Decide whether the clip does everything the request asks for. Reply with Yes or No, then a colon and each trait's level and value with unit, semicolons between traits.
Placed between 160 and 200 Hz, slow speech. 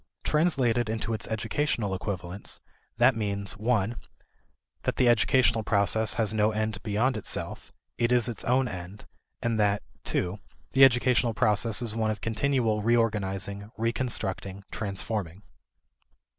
No: low, 110 Hz; slow, 130 wpm